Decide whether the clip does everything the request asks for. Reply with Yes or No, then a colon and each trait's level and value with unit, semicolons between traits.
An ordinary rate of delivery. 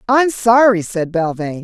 Yes: average, 145 wpm